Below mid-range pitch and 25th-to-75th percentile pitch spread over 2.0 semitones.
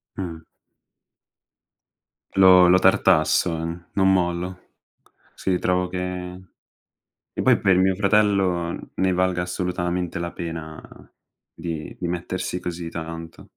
No: very low, 90 Hz; narrow, 1.4 semitones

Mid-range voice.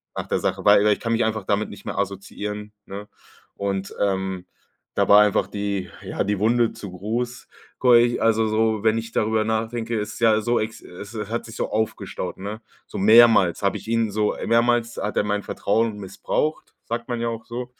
No: low, 110 Hz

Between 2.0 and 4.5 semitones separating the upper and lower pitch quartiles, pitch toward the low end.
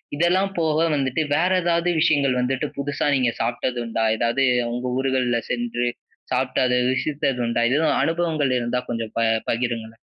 Yes: average, 4.2 semitones; low, 130 Hz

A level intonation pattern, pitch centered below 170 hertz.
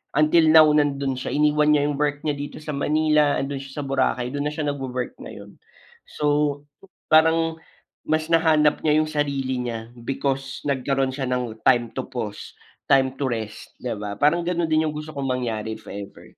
No: average, 3.0 semitones; medium, 140 Hz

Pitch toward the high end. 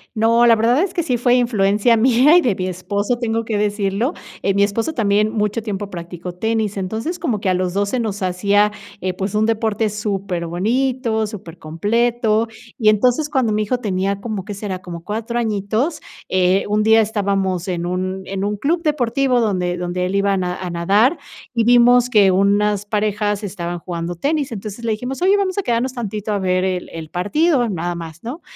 Yes: high, 210 Hz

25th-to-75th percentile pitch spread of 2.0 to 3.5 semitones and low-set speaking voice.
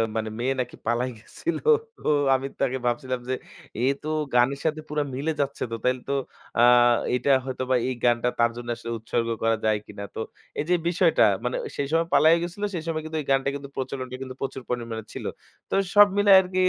No: average, 4.1 semitones; low, 130 Hz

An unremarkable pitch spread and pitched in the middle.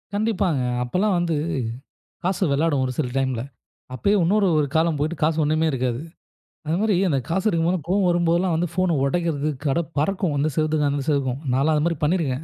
Yes: average, 3.7 semitones; medium, 160 Hz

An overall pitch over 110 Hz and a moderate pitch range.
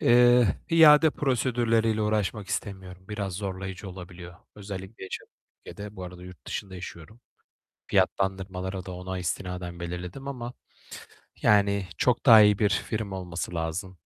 No: very low, 95 Hz; average, 3.2 semitones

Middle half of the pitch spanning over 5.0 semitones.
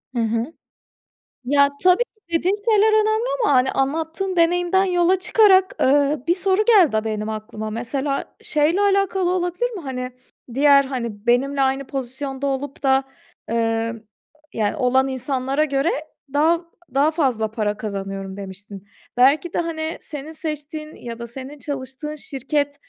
Yes: wide, 5.5 semitones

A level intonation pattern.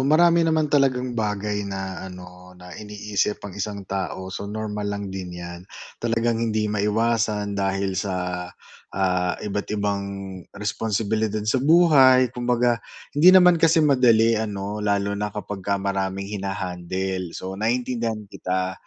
No: average, 3.3 semitones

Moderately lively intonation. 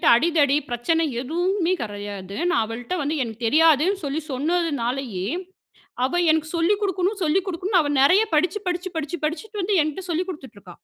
No: wide, 5.8 semitones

